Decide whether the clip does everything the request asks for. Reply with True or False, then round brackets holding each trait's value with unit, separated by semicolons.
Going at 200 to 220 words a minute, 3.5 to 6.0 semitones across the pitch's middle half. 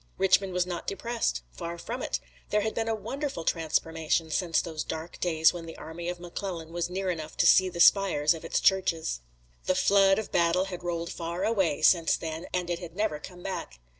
False (205 wpm; 2.7 semitones)